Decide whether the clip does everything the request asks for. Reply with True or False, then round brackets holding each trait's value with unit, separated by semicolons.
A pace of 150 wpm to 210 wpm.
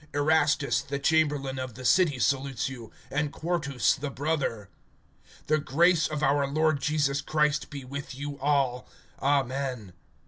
False (140 wpm)